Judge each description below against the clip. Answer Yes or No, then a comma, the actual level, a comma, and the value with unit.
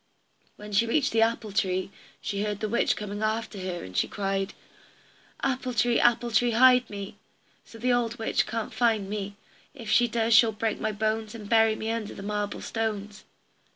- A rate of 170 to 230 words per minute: Yes, average, 190 wpm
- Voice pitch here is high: Yes, high, 220 Hz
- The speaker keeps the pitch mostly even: Yes, narrow, 2.1 semitones